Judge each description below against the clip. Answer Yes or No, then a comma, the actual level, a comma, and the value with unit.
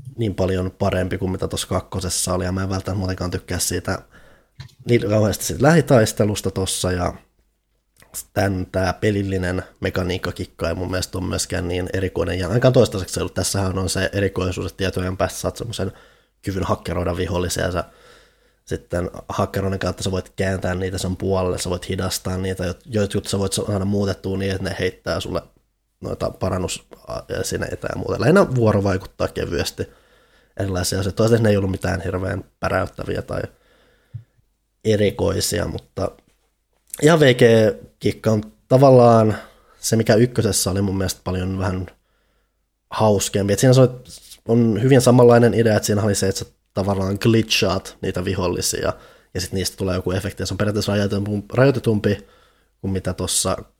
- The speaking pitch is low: Yes, very low, 95 Hz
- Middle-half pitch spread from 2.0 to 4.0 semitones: Yes, average, 2.7 semitones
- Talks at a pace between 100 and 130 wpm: No, fast, 155 wpm